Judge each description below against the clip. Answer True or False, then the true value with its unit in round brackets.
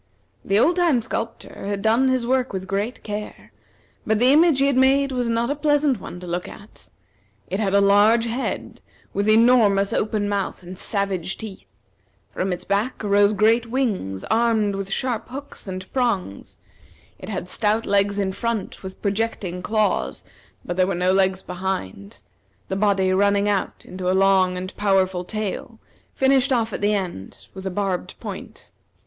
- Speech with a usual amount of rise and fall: True (3.5 semitones)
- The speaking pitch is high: True (205 Hz)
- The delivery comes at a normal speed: True (170 wpm)